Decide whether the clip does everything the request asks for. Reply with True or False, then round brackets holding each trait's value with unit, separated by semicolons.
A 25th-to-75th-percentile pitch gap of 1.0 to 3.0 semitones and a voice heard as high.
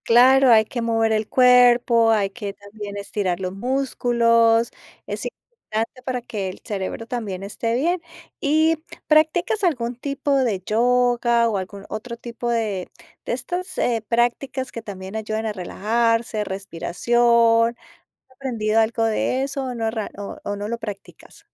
True (2.7 semitones; 230 Hz)